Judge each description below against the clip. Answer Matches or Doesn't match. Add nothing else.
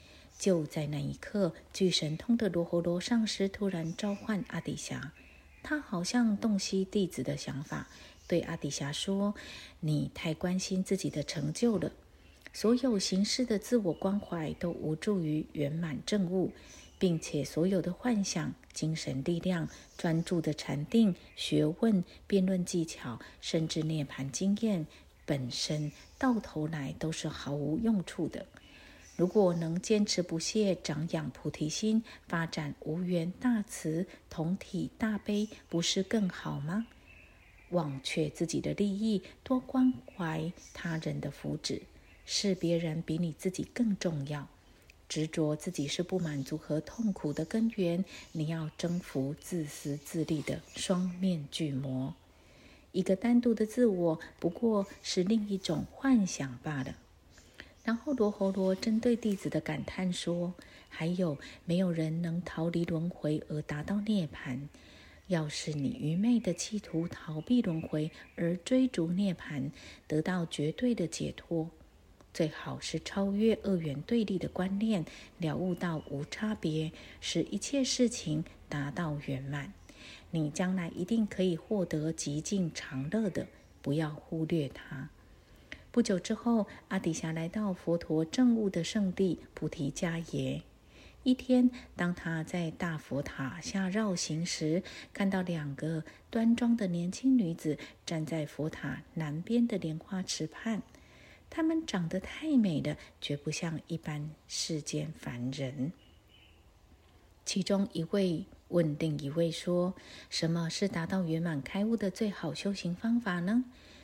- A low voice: Doesn't match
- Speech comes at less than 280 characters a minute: Matches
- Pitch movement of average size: Matches